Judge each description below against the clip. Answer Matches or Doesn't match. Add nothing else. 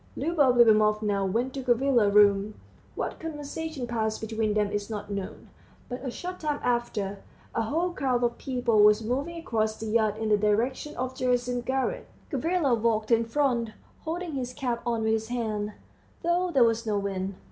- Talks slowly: Doesn't match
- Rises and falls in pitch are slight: Doesn't match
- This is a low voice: Doesn't match